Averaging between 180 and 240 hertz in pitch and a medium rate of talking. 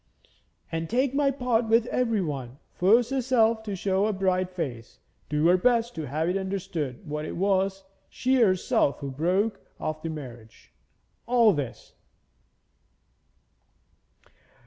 No: high, 190 Hz; slow, 130 wpm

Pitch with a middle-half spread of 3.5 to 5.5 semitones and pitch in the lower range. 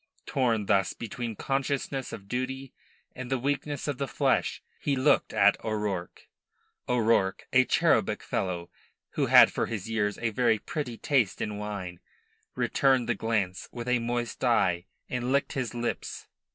Yes: average, 4.1 semitones; low, 120 Hz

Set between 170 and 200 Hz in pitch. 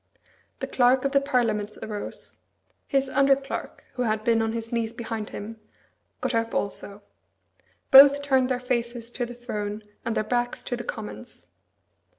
No: high, 240 Hz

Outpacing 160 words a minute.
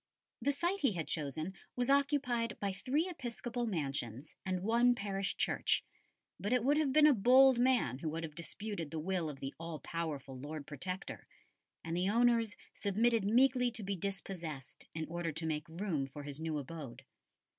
Yes: average, 175 wpm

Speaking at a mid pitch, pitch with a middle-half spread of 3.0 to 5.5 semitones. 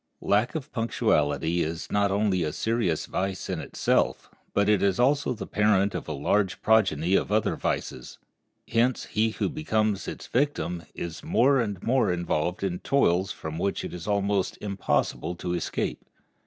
No: low, 100 Hz; average, 4.1 semitones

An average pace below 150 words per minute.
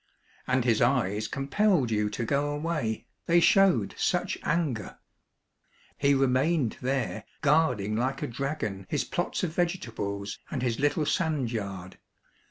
Yes: average, 140 wpm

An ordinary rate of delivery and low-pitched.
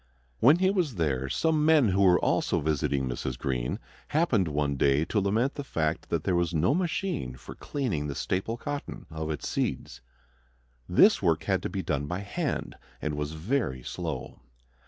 Yes: average, 175 wpm; very low, 90 Hz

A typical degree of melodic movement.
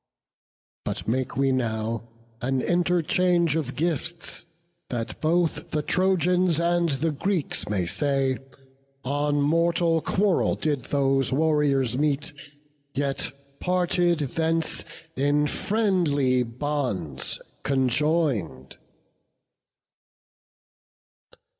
Yes: average, 4.4 semitones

